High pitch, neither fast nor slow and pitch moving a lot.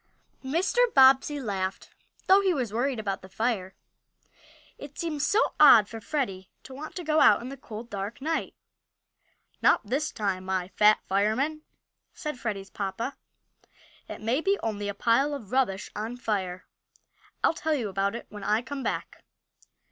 Yes: high, 230 Hz; average, 165 wpm; wide, 5.9 semitones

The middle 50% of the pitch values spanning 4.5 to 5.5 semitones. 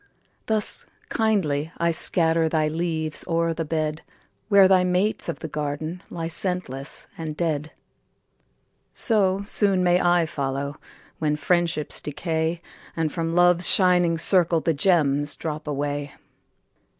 No: average, 2.8 semitones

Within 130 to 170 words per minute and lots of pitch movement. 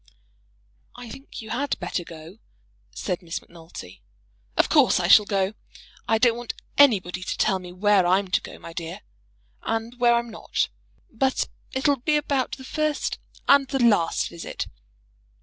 Yes: average, 160 wpm; wide, 6.2 semitones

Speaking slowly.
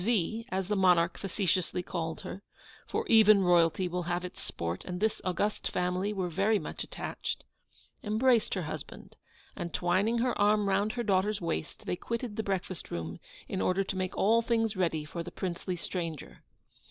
No: average, 175 wpm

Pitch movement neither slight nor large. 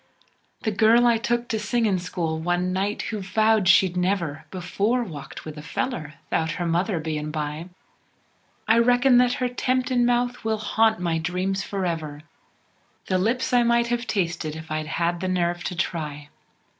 No: wide, 5.8 semitones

